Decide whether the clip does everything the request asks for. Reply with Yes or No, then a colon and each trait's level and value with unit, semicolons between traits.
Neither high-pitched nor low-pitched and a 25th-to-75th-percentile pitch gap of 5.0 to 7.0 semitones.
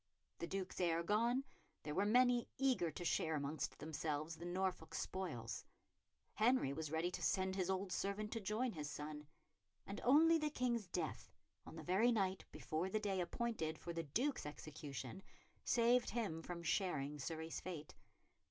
Yes: medium, 180 Hz; wide, 5.5 semitones